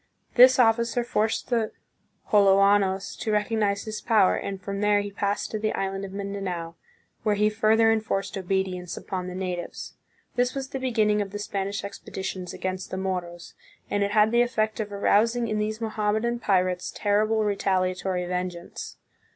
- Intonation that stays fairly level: Yes, narrow, 2.3 semitones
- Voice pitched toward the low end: No, high, 205 Hz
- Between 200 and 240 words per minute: No, average, 165 wpm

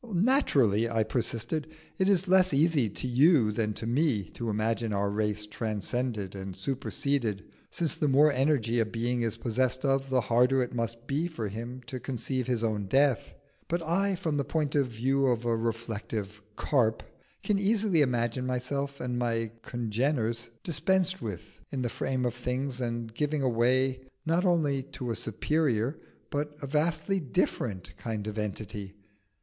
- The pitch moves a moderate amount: Yes, average, 4.3 semitones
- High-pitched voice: No, low, 125 Hz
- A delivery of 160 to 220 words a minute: Yes, average, 165 wpm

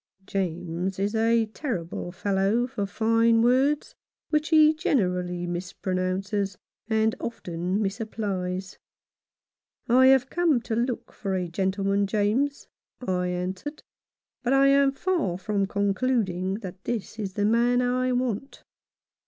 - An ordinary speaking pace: No, slow, 125 wpm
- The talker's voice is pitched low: No, high, 210 Hz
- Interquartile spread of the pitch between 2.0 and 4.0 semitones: No, average, 4.8 semitones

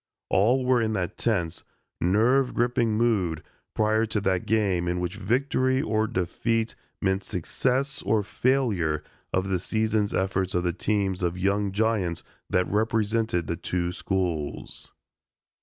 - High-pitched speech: No, low, 100 Hz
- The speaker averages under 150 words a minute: Yes, average, 140 wpm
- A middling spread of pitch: Yes, average, 3.8 semitones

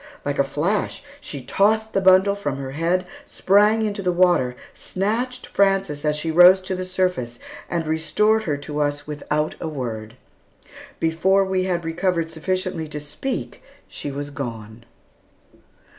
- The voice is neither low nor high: Yes, medium, 170 Hz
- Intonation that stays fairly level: No, average, 4.9 semitones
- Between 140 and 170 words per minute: Yes, average, 150 wpm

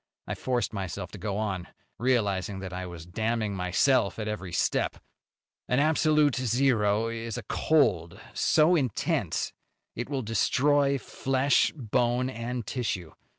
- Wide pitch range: No, average, 4.9 semitones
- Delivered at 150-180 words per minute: No, slow, 135 wpm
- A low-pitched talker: Yes, low, 115 Hz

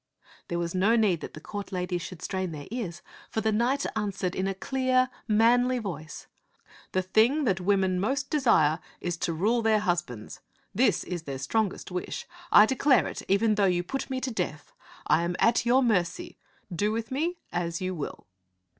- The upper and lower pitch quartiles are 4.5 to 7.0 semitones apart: Yes, average, 5.1 semitones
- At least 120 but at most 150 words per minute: No, average, 190 wpm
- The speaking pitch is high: Yes, high, 200 Hz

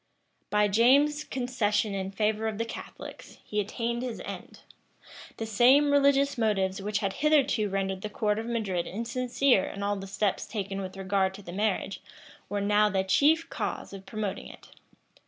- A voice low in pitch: No, high, 210 Hz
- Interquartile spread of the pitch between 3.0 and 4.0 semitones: Yes, average, 3.5 semitones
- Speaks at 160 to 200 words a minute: Yes, average, 170 wpm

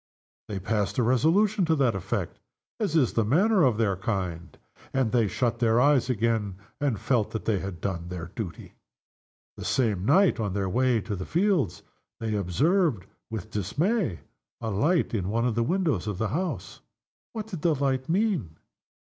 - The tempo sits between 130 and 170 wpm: No, average, 180 wpm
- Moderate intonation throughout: No, wide, 7.4 semitones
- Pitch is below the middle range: Yes, low, 115 Hz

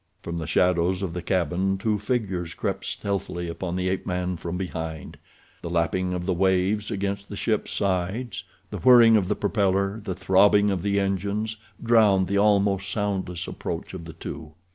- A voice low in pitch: Yes, very low, 95 Hz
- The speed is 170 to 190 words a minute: Yes, average, 175 wpm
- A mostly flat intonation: Yes, narrow, 2.2 semitones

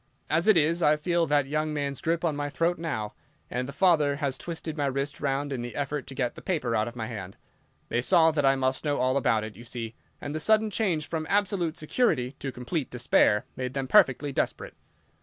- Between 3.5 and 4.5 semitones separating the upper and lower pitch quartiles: Yes, average, 4.1 semitones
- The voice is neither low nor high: Yes, medium, 145 Hz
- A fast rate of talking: Yes, fast, 225 wpm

